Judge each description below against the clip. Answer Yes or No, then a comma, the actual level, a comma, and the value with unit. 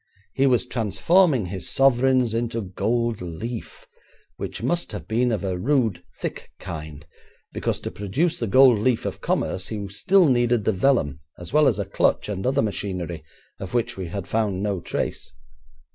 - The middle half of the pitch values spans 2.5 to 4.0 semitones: No, average, 4.9 semitones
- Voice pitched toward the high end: No, low, 110 Hz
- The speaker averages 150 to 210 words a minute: Yes, average, 170 wpm